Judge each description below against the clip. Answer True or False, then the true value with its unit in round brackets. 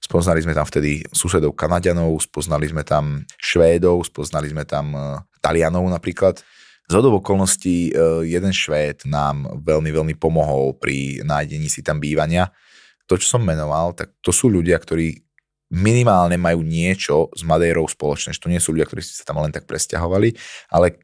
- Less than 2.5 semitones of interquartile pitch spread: False (2.8 semitones)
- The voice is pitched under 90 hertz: True (80 Hz)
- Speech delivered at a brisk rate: False (155 wpm)